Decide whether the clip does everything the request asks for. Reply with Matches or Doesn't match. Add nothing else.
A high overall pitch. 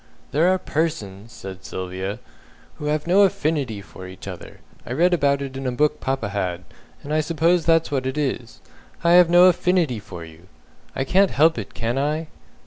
Doesn't match